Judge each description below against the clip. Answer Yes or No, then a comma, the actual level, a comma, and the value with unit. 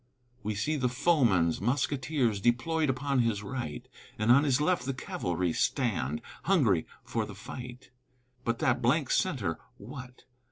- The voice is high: No, low, 125 Hz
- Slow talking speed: No, average, 145 wpm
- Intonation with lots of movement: No, average, 4.7 semitones